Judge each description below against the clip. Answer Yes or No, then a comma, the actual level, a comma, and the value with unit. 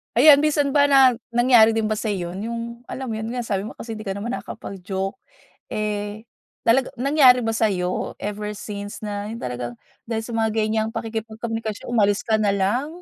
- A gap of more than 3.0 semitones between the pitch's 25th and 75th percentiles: No, average, 2.7 semitones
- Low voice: No, high, 220 Hz